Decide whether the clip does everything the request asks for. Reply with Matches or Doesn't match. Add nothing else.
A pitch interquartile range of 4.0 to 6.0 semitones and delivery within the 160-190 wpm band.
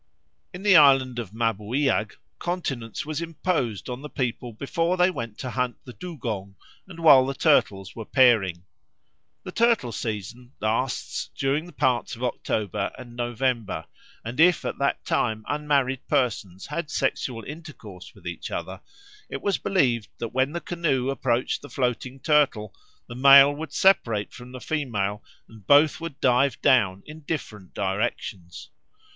Doesn't match